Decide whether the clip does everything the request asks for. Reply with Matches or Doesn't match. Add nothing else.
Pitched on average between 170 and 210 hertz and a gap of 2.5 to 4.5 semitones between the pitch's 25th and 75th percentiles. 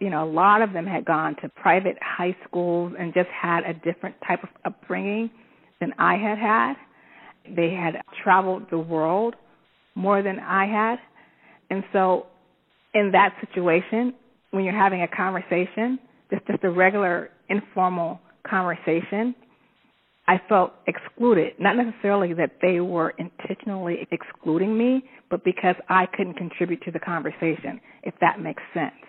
Matches